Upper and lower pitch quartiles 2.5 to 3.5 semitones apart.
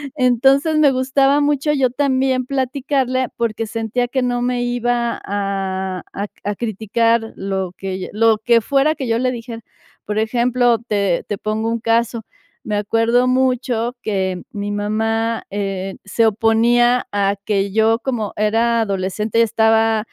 Yes: average, 3.2 semitones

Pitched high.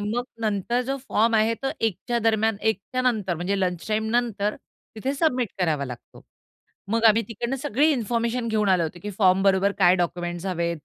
Yes: high, 215 Hz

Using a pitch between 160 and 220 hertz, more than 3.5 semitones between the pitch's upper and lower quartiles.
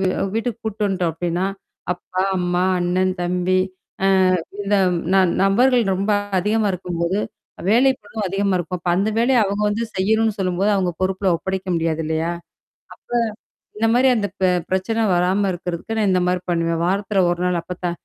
No: medium, 185 Hz; average, 2.7 semitones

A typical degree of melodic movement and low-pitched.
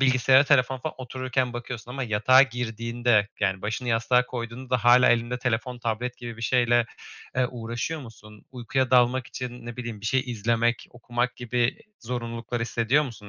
No: narrow, 1.6 semitones; low, 120 Hz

